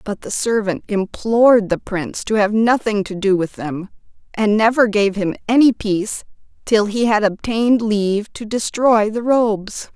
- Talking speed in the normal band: Yes, average, 170 wpm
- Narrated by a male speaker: No, female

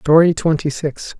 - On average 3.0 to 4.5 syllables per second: Yes, 4.4 syllables/s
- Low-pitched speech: No, medium, 155 Hz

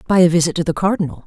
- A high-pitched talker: No, medium, 170 Hz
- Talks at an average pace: No, fast, 285 wpm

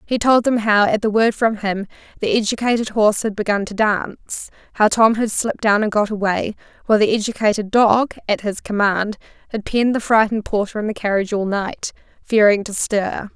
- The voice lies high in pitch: Yes, high, 215 Hz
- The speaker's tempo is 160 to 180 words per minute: No, average, 200 wpm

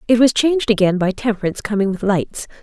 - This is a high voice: Yes, high, 210 Hz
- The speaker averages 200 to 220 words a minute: Yes, fast, 205 wpm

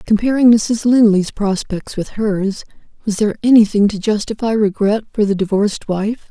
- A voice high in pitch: Yes, high, 210 Hz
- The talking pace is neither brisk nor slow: Yes, average, 150 wpm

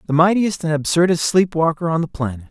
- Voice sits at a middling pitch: Yes, medium, 165 Hz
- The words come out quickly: Yes, fast, 215 wpm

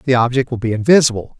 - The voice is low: Yes, low, 125 Hz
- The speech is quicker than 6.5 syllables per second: Yes, 6.7 syllables/s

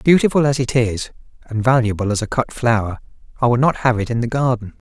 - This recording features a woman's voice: No, male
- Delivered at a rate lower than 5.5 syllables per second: No, 6.0 syllables/s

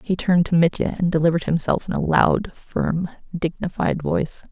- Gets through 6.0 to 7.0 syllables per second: No, 5.5 syllables/s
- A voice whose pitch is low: No, medium, 170 Hz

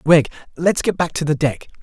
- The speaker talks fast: Yes, fast, 230 wpm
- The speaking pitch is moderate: Yes, medium, 155 Hz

